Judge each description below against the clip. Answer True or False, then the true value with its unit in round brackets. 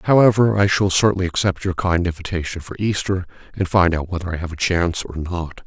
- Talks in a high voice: False (90 Hz)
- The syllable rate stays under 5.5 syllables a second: False (5.9 syllables/s)